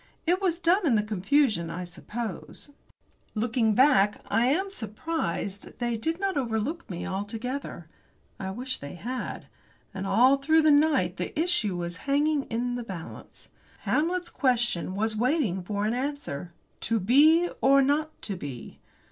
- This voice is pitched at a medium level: No, high, 245 Hz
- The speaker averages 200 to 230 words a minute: No, average, 150 wpm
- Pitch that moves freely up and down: Yes, wide, 6.8 semitones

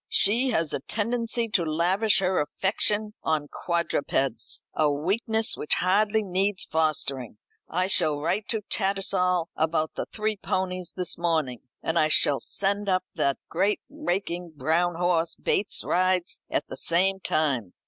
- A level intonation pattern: No, average, 4.2 semitones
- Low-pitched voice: No, medium, 180 Hz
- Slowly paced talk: No, average, 145 wpm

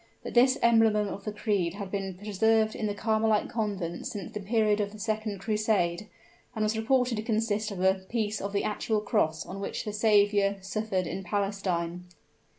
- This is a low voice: No, high, 210 Hz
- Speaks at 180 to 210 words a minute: Yes, average, 185 wpm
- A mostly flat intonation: Yes, narrow, 1.9 semitones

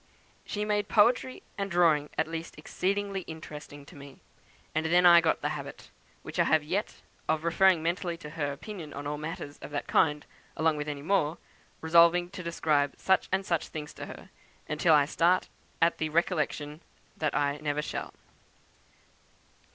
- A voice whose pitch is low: No, medium, 160 Hz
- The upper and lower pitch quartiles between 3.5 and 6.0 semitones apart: No, average, 3.1 semitones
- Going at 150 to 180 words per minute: Yes, average, 170 wpm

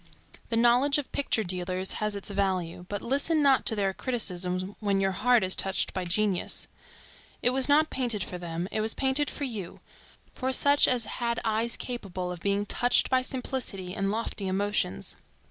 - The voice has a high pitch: Yes, high, 210 Hz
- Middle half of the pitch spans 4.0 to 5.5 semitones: Yes, average, 5.1 semitones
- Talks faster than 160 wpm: Yes, average, 180 wpm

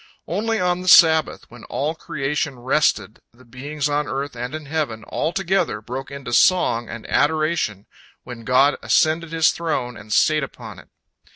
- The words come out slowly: No, average, 165 wpm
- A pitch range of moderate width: Yes, average, 4.5 semitones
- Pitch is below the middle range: No, medium, 145 Hz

